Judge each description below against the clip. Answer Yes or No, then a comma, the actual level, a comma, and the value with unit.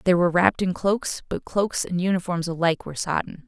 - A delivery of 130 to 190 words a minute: No, fast, 205 wpm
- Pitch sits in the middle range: Yes, medium, 180 Hz